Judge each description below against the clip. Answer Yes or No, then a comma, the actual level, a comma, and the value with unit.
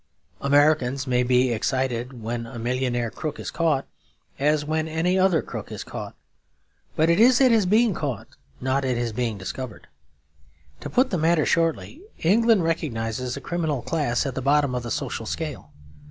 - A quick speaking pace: No, average, 170 wpm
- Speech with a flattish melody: No, average, 5.1 semitones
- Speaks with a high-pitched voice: No, medium, 140 Hz